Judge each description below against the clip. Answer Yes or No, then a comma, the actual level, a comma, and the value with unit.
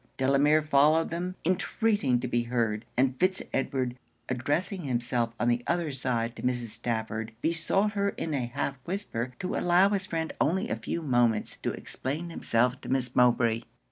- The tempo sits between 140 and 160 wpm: No, average, 170 wpm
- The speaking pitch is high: No, low, 135 Hz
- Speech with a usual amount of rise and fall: No, wide, 5.9 semitones